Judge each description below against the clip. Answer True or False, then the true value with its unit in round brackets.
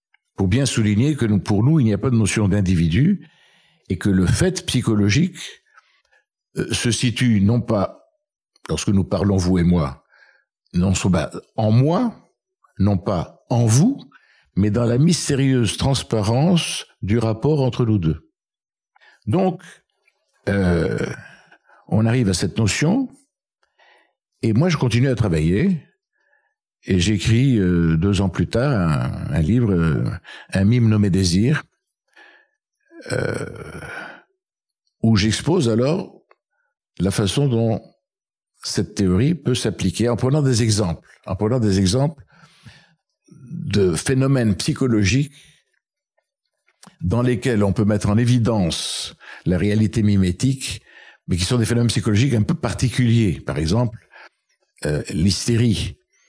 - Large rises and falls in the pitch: True (6.1 semitones)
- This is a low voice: True (115 Hz)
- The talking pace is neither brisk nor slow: False (125 wpm)